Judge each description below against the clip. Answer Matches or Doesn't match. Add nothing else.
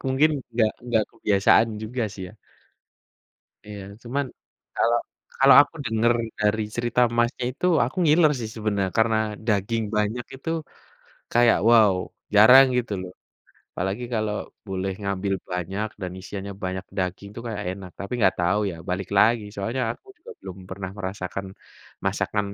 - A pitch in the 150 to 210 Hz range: Doesn't match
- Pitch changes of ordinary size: Matches